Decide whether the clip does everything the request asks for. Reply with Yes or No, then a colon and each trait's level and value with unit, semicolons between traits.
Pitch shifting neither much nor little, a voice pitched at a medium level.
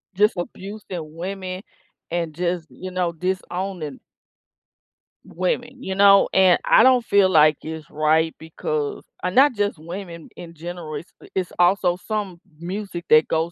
Yes: average, 3.2 semitones; medium, 180 Hz